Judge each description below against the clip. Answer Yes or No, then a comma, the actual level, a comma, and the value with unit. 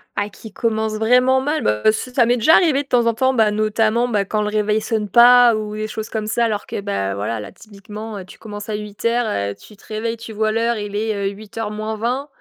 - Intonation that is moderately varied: No, narrow, 2.0 semitones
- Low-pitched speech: No, high, 215 Hz